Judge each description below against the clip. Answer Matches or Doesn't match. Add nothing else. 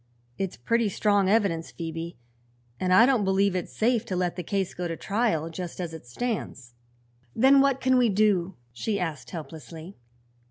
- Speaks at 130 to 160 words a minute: Doesn't match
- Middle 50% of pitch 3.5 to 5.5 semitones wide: Matches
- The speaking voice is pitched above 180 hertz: Matches